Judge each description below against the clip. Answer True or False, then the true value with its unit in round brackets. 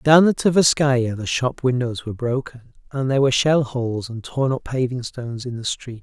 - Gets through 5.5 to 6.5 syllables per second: False (5.1 syllables/s)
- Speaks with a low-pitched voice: True (130 Hz)